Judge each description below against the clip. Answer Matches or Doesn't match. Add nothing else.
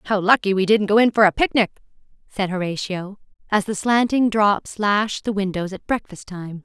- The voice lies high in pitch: Matches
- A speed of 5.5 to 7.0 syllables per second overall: Doesn't match